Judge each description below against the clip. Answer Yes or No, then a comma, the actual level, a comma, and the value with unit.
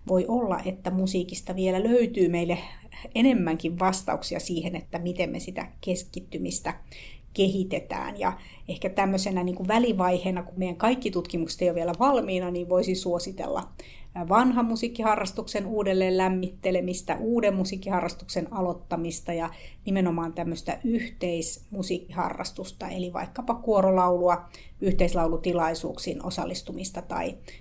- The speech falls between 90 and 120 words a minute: Yes, average, 110 wpm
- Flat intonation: Yes, narrow, 2.3 semitones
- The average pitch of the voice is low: No, medium, 185 Hz